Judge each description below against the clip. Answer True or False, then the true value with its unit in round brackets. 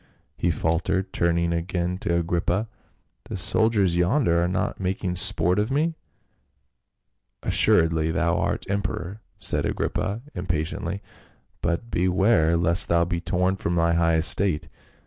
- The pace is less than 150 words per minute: True (140 wpm)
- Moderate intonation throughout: False (2.3 semitones)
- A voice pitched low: True (90 Hz)